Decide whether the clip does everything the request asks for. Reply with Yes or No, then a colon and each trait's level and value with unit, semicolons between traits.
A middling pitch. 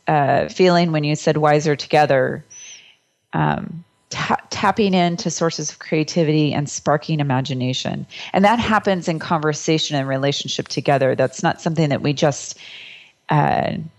Yes: medium, 155 Hz